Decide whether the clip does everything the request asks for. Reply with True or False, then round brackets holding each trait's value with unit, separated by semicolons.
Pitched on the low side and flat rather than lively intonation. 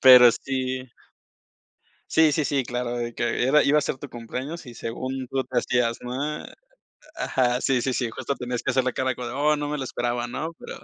True (130 Hz; 2.2 semitones)